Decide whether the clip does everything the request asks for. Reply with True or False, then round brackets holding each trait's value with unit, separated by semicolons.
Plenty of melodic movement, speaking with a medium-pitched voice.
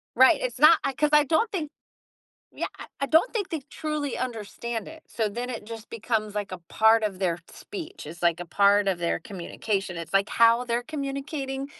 False (6.2 semitones; 235 Hz)